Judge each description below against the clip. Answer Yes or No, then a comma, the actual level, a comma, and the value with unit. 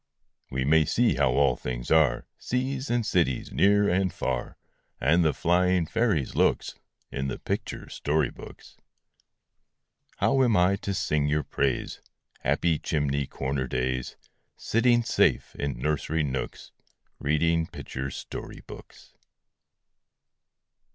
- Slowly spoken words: Yes, slow, 125 wpm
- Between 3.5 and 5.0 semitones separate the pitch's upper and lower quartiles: No, wide, 5.4 semitones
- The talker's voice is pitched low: Yes, very low, 75 Hz